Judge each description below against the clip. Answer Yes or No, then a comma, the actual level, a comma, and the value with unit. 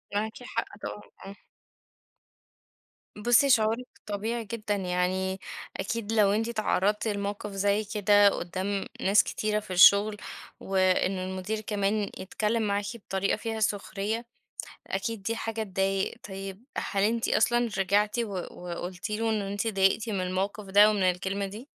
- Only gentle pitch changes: Yes, narrow, 2.1 semitones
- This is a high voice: Yes, high, 205 Hz